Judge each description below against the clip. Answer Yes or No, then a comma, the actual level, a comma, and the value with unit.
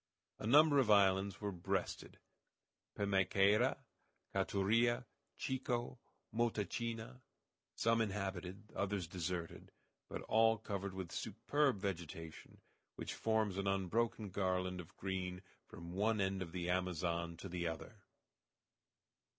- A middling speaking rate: No, slow, 110 wpm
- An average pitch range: Yes, average, 3.4 semitones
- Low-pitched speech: Yes, low, 100 Hz